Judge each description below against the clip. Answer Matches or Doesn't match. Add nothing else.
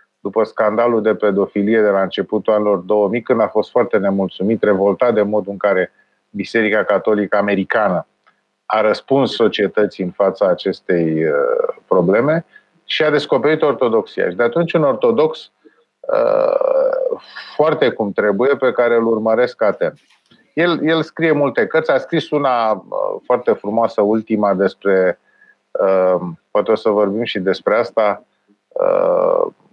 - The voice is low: Matches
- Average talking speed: Matches